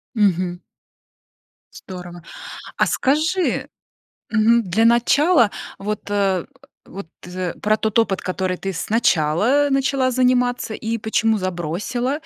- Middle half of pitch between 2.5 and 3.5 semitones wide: No, average, 5.0 semitones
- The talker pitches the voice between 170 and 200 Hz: No, high, 215 Hz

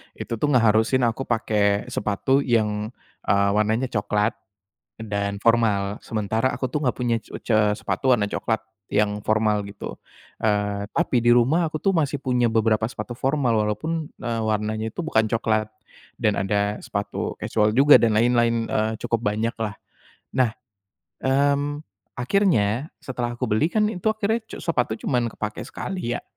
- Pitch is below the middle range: Yes, low, 115 Hz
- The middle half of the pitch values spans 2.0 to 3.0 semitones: No, average, 3.6 semitones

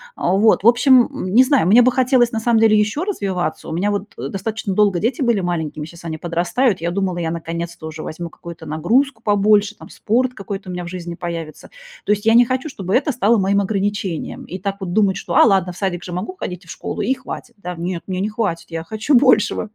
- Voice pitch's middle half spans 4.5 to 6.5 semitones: Yes, average, 4.8 semitones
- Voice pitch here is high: Yes, high, 200 Hz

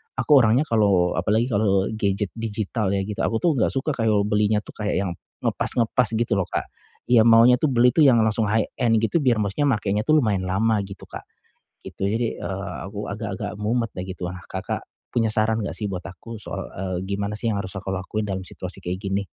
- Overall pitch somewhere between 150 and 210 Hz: No, low, 105 Hz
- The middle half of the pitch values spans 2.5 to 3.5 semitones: Yes, average, 2.8 semitones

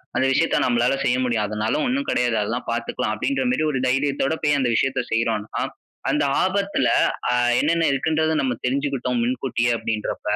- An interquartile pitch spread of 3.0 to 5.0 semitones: Yes, average, 3.7 semitones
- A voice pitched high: No, low, 130 Hz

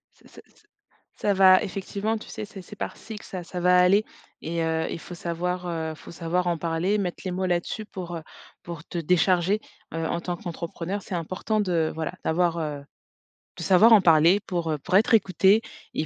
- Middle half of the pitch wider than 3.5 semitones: No, average, 2.7 semitones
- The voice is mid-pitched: Yes, medium, 180 Hz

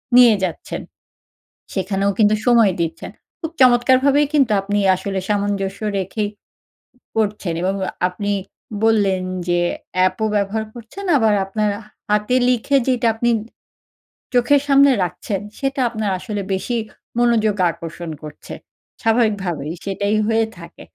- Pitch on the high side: Yes, high, 215 Hz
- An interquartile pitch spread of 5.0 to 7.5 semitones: No, average, 3.7 semitones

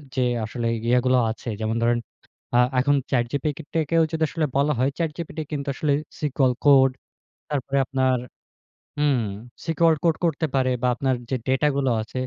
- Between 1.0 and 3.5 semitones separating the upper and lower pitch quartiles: Yes, average, 2.9 semitones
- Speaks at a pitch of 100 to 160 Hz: Yes, low, 135 Hz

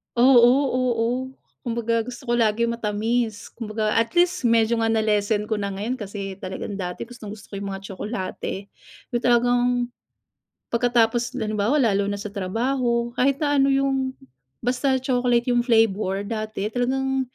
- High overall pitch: Yes, high, 230 Hz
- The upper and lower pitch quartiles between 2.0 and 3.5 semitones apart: Yes, average, 2.8 semitones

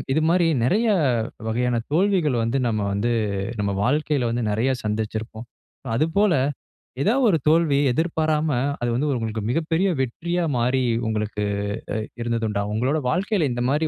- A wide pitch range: Yes, wide, 5.9 semitones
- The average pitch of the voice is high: No, low, 130 Hz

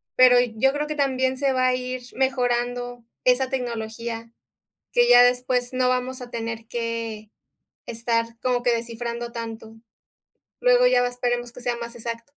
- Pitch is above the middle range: Yes, high, 245 Hz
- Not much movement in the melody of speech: Yes, narrow, 1.6 semitones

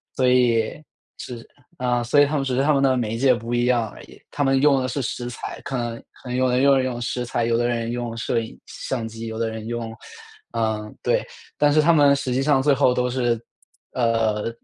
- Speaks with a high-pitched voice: No, low, 125 Hz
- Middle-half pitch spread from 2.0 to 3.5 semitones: Yes, narrow, 2.5 semitones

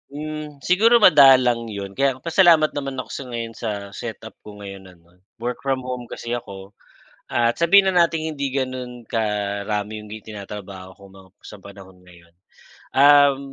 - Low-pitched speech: Yes, low, 120 Hz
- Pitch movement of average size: No, wide, 5.7 semitones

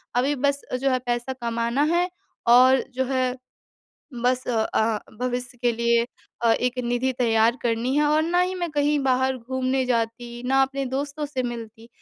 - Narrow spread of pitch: Yes, narrow, 2.1 semitones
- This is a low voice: No, very high, 255 Hz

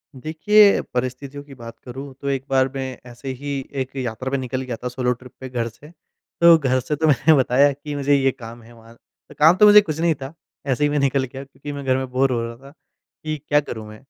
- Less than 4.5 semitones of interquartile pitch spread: Yes, narrow, 2.4 semitones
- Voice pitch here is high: No, low, 135 Hz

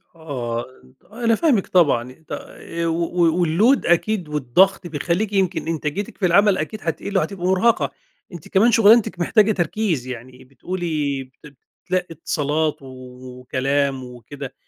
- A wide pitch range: Yes, wide, 6.0 semitones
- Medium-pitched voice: Yes, medium, 165 Hz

